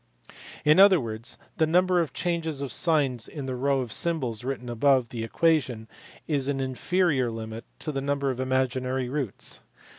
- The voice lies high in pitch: No, low, 135 Hz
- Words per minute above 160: Yes, average, 170 wpm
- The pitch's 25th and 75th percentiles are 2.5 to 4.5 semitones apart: Yes, average, 4.0 semitones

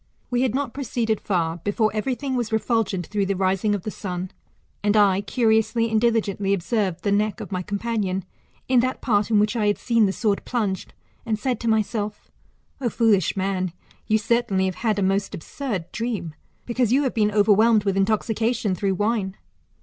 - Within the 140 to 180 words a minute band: No, average, 190 wpm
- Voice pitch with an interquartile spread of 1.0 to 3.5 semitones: Yes, average, 2.9 semitones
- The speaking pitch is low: No, high, 210 Hz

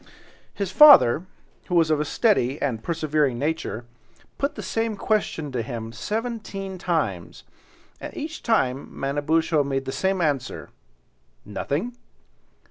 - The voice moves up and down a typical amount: No, wide, 6.6 semitones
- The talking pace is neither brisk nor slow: No, slow, 125 wpm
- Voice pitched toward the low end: No, medium, 155 Hz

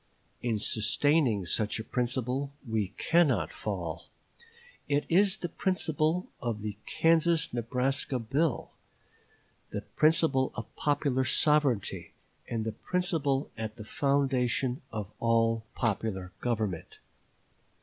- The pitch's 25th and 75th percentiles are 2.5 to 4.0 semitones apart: No, average, 5.0 semitones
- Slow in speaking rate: Yes, slow, 110 wpm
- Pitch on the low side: Yes, low, 125 Hz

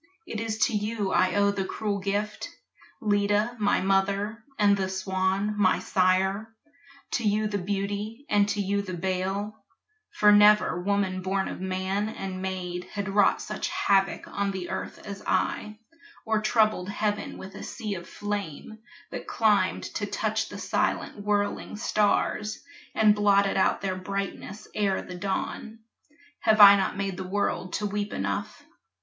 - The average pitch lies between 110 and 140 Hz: No, high, 200 Hz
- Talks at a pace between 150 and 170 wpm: Yes, average, 155 wpm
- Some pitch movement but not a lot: No, narrow, 1.7 semitones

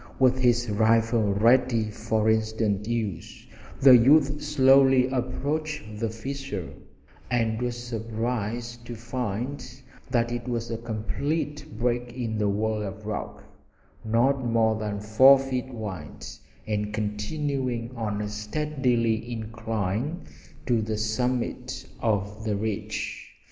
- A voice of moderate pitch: No, low, 115 Hz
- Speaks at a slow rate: Yes, slow, 120 wpm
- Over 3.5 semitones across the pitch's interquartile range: No, average, 2.9 semitones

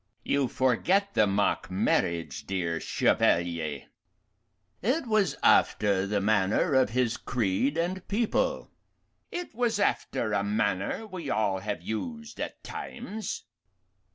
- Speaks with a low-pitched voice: Yes, low, 115 Hz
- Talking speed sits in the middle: No, slow, 120 wpm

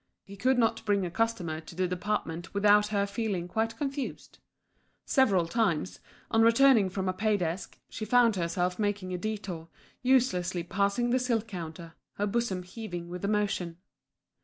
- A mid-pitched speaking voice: No, high, 200 Hz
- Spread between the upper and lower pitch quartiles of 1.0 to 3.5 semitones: No, average, 4.0 semitones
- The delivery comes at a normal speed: Yes, average, 160 wpm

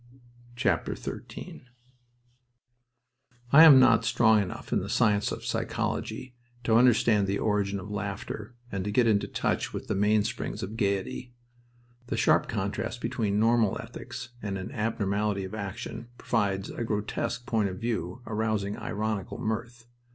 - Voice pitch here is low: Yes, low, 105 Hz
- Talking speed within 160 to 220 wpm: No, average, 140 wpm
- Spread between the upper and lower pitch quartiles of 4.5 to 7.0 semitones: No, narrow, 2.4 semitones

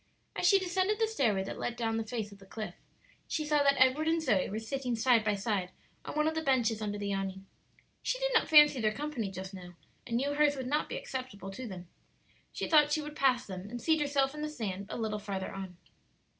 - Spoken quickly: Yes, fast, 240 wpm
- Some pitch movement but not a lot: No, wide, 6.6 semitones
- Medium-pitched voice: No, high, 245 Hz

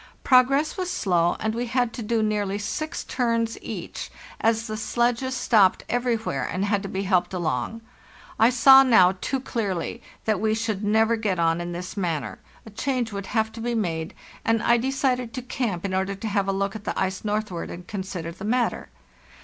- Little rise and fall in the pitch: No, average, 3.8 semitones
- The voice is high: Yes, high, 215 Hz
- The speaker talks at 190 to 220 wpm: Yes, average, 195 wpm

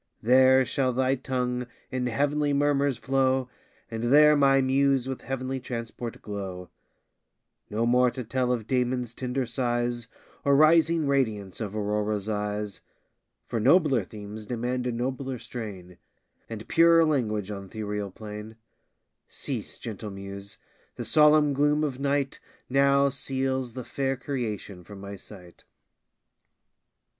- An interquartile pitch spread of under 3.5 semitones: No, average, 4.2 semitones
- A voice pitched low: Yes, low, 125 Hz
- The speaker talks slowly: Yes, slow, 130 wpm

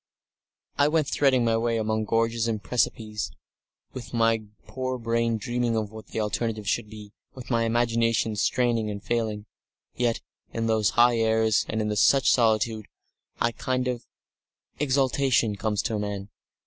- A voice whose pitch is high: No, low, 115 Hz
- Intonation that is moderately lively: No, narrow, 1.7 semitones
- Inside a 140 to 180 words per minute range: Yes, average, 150 wpm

